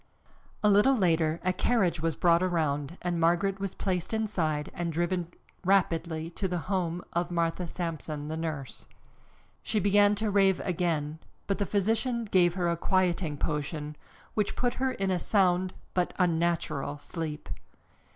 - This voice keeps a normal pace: Yes, average, 150 wpm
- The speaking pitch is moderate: Yes, medium, 175 Hz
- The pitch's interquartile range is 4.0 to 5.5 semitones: No, average, 3.1 semitones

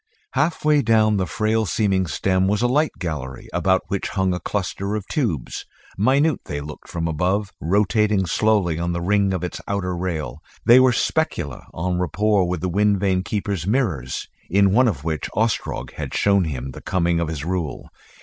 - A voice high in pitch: No, very low, 95 Hz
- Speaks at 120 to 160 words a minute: No, average, 185 wpm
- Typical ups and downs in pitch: Yes, average, 3.8 semitones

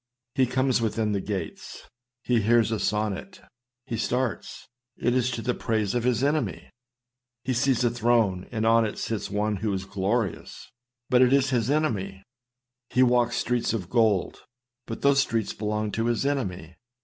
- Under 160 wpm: No, average, 170 wpm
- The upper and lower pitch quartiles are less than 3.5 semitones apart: Yes, average, 3.1 semitones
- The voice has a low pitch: Yes, low, 115 Hz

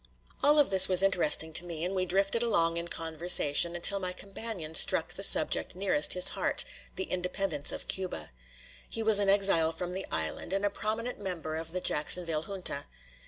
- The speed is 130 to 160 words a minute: No, average, 185 wpm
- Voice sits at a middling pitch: Yes, medium, 180 Hz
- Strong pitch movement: No, average, 3.2 semitones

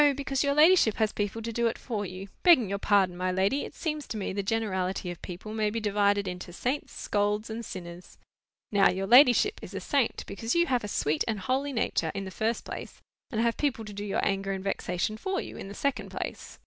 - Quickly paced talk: Yes, fast, 230 wpm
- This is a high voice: Yes, high, 210 Hz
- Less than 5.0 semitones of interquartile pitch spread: Yes, average, 4.0 semitones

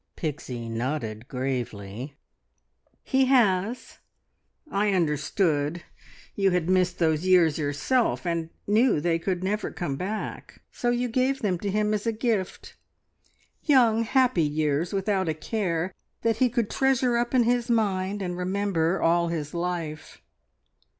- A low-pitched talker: No, medium, 185 Hz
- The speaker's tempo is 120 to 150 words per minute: Yes, slow, 135 wpm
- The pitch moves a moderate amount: No, wide, 5.9 semitones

